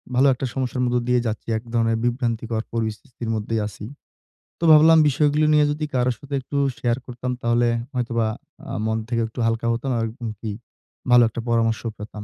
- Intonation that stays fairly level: Yes, narrow, 2.0 semitones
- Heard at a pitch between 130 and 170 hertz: No, low, 120 Hz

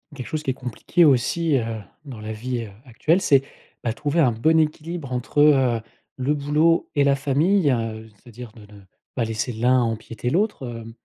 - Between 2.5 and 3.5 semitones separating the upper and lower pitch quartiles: No, average, 4.6 semitones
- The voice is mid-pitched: No, low, 130 Hz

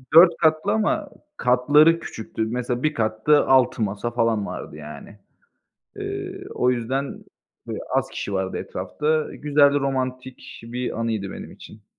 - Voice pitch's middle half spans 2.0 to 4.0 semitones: No, average, 4.7 semitones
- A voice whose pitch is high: No, low, 125 Hz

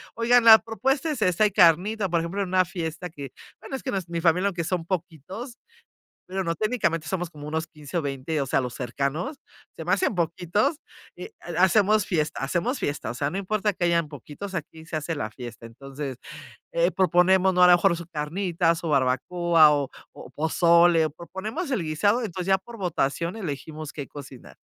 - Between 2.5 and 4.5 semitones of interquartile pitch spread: Yes, average, 4.0 semitones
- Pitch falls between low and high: Yes, medium, 170 Hz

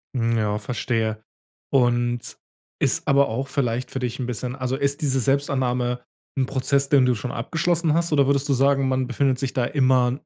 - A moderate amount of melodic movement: No, narrow, 2.3 semitones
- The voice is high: No, low, 130 Hz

